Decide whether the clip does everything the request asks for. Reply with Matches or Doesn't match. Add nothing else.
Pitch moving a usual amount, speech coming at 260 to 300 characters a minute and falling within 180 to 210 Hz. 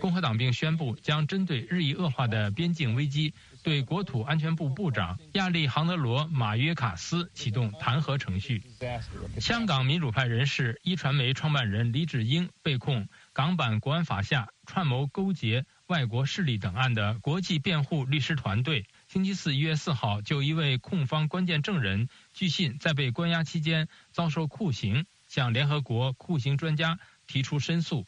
Doesn't match